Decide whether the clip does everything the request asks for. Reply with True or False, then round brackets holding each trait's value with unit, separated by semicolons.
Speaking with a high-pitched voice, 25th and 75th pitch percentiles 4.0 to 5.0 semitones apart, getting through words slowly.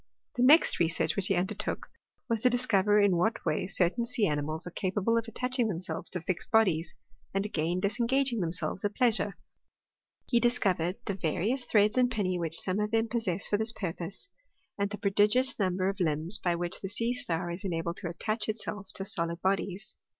False (200 Hz; 4.3 semitones; 190 wpm)